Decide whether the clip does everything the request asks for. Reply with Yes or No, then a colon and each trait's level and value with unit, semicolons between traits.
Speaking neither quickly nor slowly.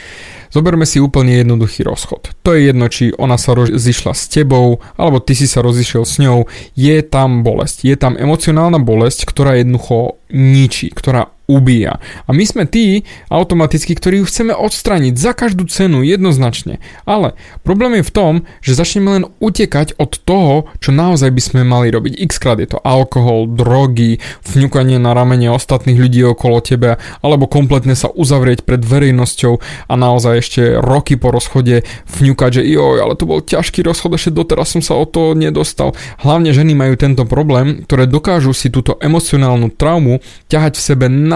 No: fast, 170 wpm